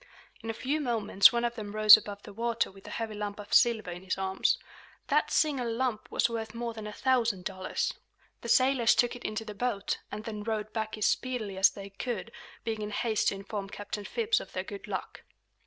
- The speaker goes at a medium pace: No, fast, 220 wpm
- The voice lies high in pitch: Yes, high, 220 Hz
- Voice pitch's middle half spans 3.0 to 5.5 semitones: No, narrow, 2.6 semitones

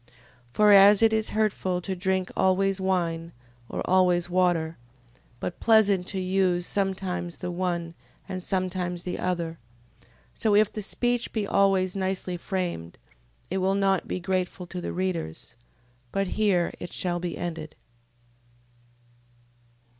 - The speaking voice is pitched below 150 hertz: No, medium, 185 Hz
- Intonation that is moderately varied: No, narrow, 1.8 semitones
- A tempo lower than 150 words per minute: Yes, slow, 135 wpm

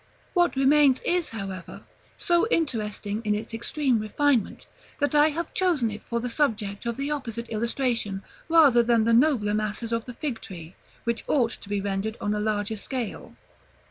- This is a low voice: No, high, 235 Hz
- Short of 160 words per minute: No, average, 175 wpm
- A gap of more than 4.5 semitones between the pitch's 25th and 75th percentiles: Yes, average, 5.2 semitones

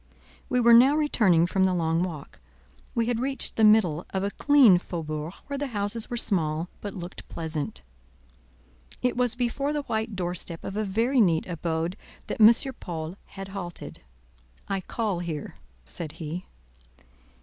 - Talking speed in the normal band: Yes, average, 160 wpm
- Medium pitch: No, high, 195 Hz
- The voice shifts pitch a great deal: Yes, wide, 5.7 semitones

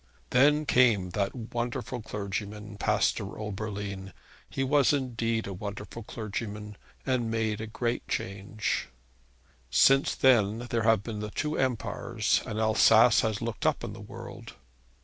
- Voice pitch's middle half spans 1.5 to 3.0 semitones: Yes, average, 2.7 semitones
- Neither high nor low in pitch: No, low, 110 Hz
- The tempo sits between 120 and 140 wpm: Yes, slow, 135 wpm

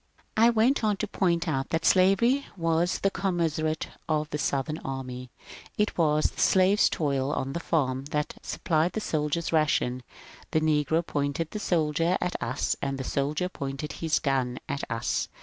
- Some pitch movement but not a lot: Yes, average, 4.2 semitones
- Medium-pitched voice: Yes, medium, 155 Hz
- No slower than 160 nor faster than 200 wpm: Yes, average, 165 wpm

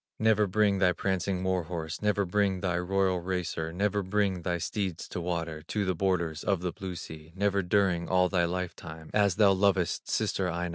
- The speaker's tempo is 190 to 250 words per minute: Yes, average, 195 wpm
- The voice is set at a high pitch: No, very low, 90 Hz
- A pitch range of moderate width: No, narrow, 2.2 semitones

